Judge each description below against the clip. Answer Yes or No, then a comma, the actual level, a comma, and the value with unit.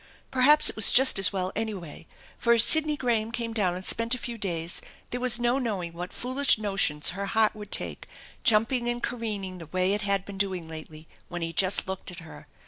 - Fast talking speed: Yes, fast, 220 wpm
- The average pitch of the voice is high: Yes, high, 205 Hz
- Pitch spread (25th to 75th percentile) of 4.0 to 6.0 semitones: Yes, average, 4.5 semitones